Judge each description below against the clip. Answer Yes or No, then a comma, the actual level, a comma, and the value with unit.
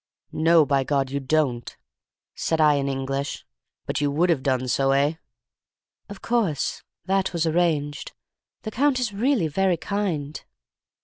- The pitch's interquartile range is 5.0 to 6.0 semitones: Yes, average, 5.3 semitones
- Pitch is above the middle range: No, medium, 155 Hz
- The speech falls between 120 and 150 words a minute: Yes, average, 145 wpm